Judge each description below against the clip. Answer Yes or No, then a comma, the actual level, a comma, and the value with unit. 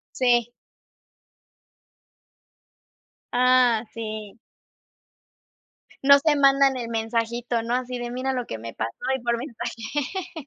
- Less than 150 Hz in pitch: No, high, 245 Hz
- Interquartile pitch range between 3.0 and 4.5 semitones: No, narrow, 2.5 semitones